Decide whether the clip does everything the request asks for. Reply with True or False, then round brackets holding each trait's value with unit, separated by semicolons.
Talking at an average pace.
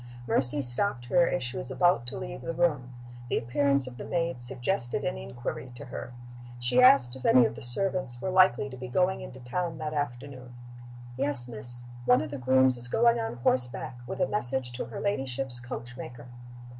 True (195 wpm)